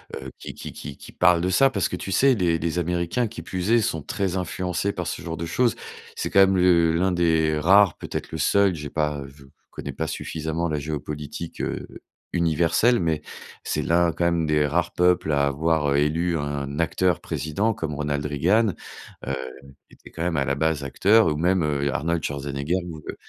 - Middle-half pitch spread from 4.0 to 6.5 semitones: No, average, 3.2 semitones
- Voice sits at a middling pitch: No, very low, 85 Hz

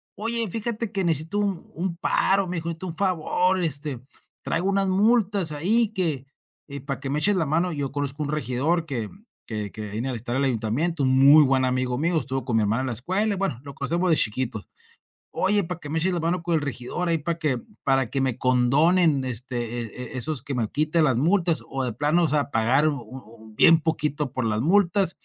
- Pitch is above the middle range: No, medium, 150 Hz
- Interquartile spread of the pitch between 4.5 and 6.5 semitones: Yes, average, 5.3 semitones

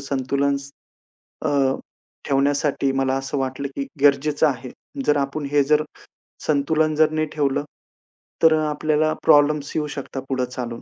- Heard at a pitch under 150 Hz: Yes, medium, 140 Hz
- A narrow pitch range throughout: Yes, narrow, 2.0 semitones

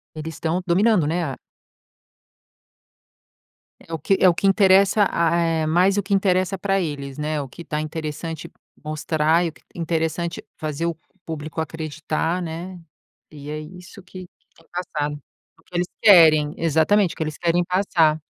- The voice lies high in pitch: No, medium, 165 Hz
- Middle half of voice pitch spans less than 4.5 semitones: Yes, average, 2.8 semitones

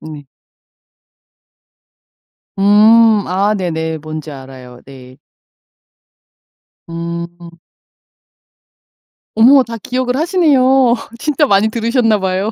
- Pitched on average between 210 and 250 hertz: No, high, 200 Hz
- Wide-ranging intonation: Yes, wide, 6.8 semitones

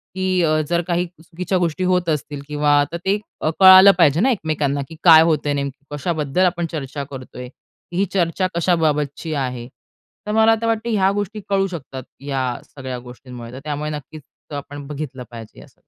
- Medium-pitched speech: Yes, medium, 155 Hz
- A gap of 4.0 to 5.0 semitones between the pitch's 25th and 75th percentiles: Yes, average, 4.6 semitones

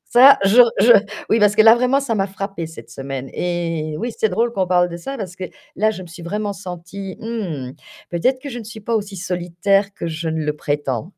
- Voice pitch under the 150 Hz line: No, high, 195 Hz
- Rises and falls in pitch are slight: No, average, 4.5 semitones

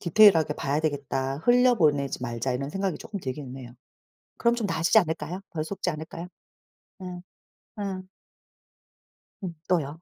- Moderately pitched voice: Yes, medium, 160 Hz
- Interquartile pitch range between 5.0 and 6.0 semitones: Yes, average, 5.3 semitones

